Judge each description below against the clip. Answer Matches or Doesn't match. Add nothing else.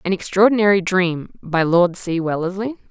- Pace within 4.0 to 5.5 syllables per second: Matches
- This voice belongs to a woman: Matches